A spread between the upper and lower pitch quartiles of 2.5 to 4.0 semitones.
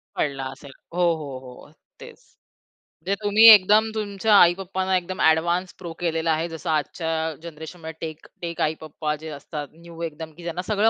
Yes: average, 2.9 semitones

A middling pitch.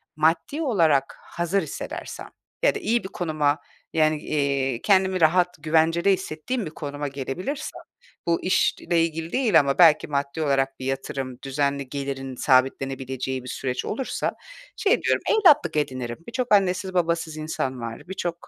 Yes: medium, 155 Hz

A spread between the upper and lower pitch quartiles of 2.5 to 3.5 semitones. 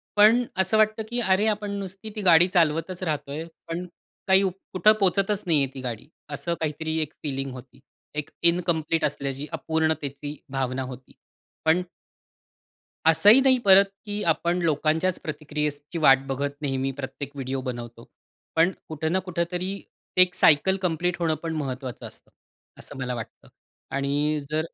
No: average, 4.9 semitones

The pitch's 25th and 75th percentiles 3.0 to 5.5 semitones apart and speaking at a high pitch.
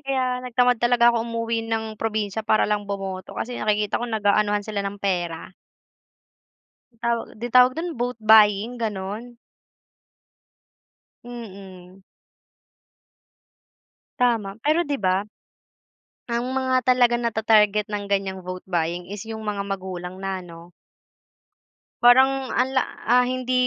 Yes: average, 3.7 semitones; high, 215 Hz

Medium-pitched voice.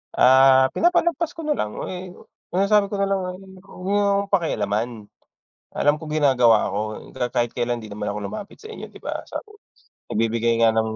No: low, 130 Hz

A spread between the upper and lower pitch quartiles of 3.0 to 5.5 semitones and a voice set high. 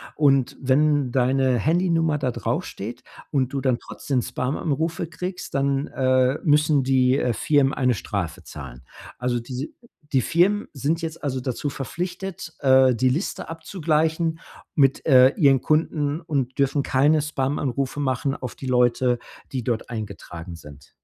No: average, 3.3 semitones; low, 135 Hz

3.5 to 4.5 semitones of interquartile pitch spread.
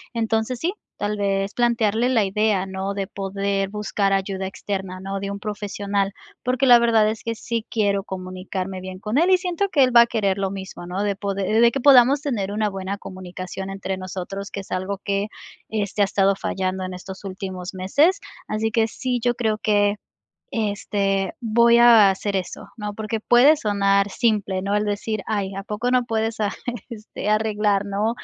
No: narrow, 2.5 semitones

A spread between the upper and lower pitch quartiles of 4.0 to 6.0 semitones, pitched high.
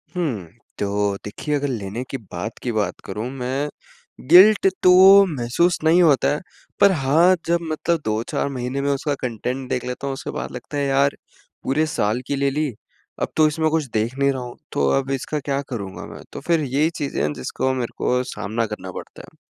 No: average, 4.5 semitones; low, 135 Hz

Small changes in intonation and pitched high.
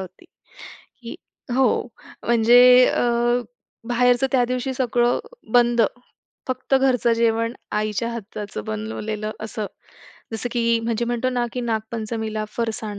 Yes: narrow, 2.1 semitones; high, 235 Hz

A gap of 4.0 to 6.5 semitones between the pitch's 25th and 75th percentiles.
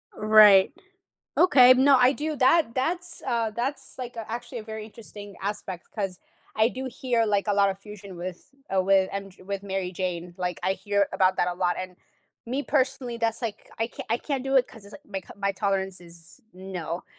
Yes: average, 4.5 semitones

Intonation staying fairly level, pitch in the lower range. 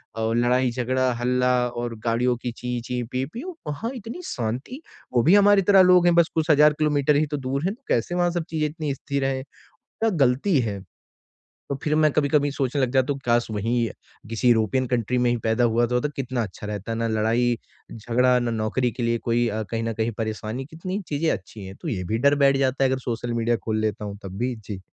No: average, 3.8 semitones; low, 125 Hz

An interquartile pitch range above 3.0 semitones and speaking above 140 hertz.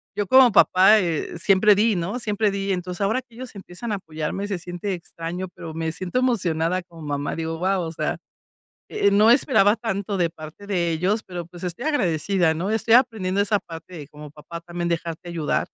Yes: average, 3.7 semitones; medium, 185 Hz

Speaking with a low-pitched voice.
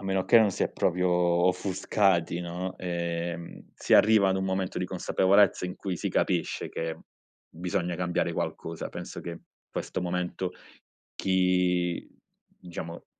Yes: very low, 90 Hz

